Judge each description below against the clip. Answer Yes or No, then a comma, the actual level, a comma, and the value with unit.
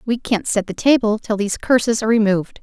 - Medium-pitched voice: No, high, 220 Hz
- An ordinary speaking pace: No, fast, 230 wpm